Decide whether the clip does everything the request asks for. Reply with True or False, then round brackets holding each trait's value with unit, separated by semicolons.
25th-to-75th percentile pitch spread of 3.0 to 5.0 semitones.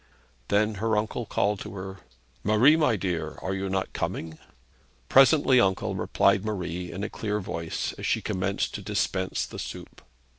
False (2.6 semitones)